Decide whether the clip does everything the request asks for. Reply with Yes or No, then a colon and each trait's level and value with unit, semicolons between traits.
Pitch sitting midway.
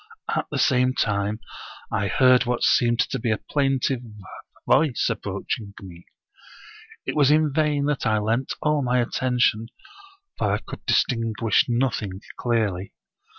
No: low, 120 Hz